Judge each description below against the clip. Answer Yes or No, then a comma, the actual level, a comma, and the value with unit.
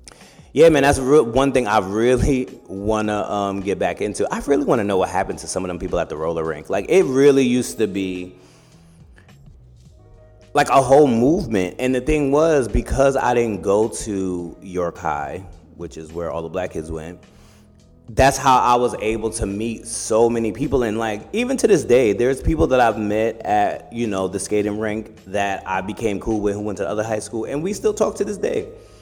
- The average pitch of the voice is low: Yes, low, 110 Hz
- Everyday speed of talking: No, fast, 215 wpm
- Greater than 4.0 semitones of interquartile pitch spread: Yes, average, 5.0 semitones